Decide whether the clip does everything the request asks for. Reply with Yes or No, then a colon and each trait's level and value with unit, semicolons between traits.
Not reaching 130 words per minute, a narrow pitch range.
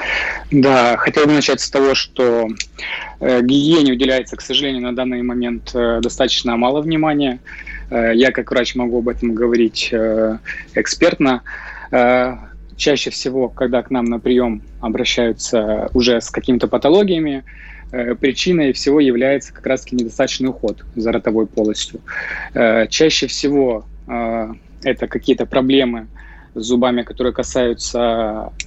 Yes: average, 115 wpm; narrow, 2.2 semitones